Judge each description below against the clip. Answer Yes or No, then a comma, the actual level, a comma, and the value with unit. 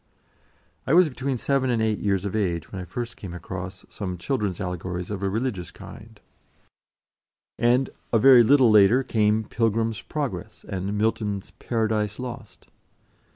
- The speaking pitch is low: Yes, low, 110 Hz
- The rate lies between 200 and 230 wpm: No, average, 150 wpm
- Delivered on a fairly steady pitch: No, average, 3.8 semitones